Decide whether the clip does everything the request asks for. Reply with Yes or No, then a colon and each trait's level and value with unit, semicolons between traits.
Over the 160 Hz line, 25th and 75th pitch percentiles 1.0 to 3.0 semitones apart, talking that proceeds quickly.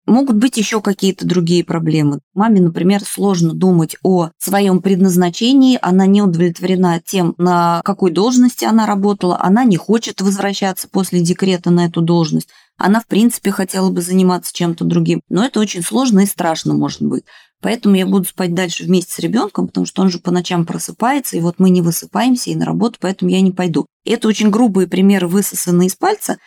Yes: medium, 185 Hz; average, 2.7 semitones; fast, 185 wpm